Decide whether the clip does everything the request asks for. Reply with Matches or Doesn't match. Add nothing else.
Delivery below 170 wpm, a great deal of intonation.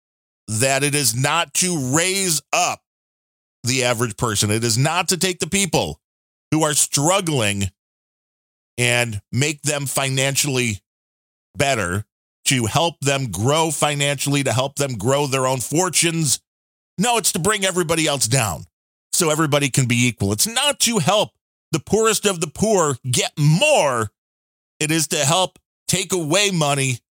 Matches